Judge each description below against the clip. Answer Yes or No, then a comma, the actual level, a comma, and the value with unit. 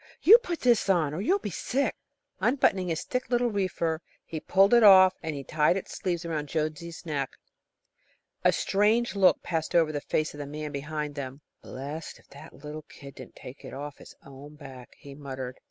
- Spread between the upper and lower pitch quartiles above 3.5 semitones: Yes, average, 5.0 semitones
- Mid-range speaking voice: Yes, medium, 155 Hz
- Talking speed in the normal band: Yes, average, 185 wpm